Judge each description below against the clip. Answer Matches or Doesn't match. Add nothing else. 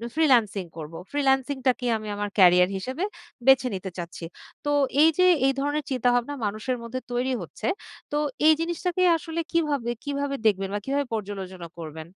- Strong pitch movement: Matches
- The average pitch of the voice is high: Matches